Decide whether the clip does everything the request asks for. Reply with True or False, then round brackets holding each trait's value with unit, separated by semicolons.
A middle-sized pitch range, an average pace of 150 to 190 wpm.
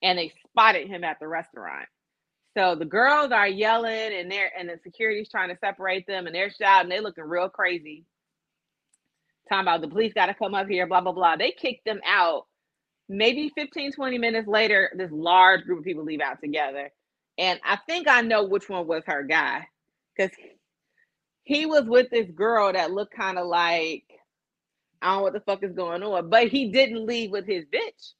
False (4.1 semitones; 200 wpm)